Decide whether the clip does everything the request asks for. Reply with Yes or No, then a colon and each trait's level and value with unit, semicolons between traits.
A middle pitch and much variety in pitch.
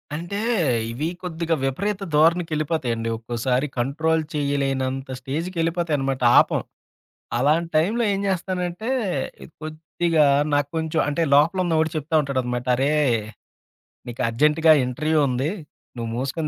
No: medium, 155 Hz; average, 3.7 semitones